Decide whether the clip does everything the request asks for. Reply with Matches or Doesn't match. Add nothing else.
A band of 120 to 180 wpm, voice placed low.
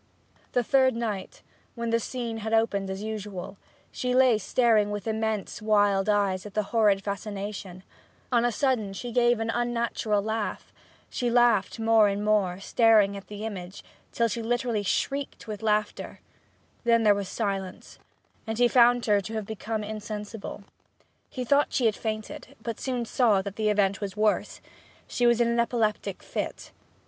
Doesn't match